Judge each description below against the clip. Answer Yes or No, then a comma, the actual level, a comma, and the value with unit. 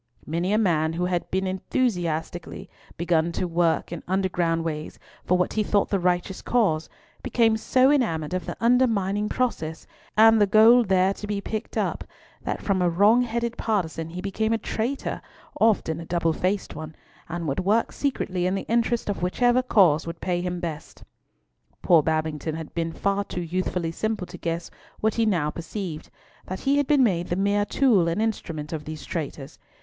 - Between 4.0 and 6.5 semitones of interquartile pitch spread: Yes, average, 4.7 semitones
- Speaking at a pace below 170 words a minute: No, average, 175 wpm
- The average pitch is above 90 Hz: Yes, medium, 185 Hz